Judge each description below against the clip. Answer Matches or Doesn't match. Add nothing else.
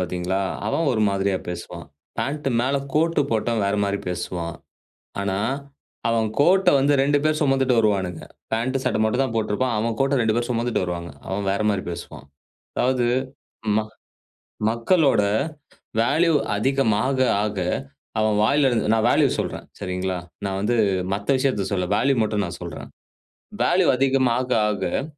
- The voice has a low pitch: Matches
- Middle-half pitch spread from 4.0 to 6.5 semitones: Matches